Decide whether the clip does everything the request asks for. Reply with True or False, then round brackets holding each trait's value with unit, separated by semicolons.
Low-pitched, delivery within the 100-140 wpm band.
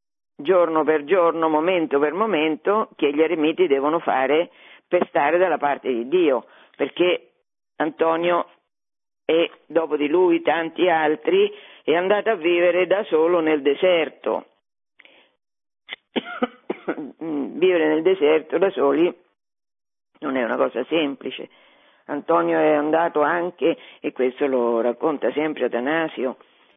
False (165 Hz; 120 wpm)